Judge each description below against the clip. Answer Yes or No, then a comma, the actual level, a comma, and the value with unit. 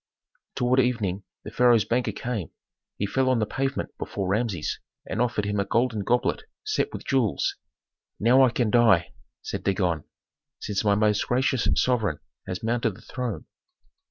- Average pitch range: Yes, average, 3.5 semitones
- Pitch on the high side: No, low, 115 Hz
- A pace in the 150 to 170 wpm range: Yes, average, 155 wpm